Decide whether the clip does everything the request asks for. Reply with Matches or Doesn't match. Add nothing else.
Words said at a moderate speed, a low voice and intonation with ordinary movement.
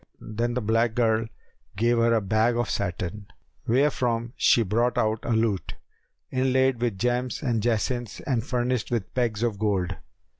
Doesn't match